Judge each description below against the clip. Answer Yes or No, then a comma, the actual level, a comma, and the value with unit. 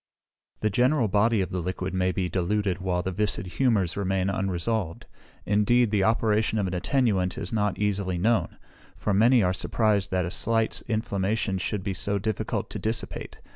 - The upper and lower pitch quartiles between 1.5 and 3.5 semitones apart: Yes, average, 2.9 semitones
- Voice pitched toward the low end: Yes, low, 100 Hz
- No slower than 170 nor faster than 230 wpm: Yes, average, 175 wpm